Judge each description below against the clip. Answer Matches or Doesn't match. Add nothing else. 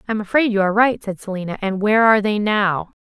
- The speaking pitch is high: Matches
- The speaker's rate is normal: Doesn't match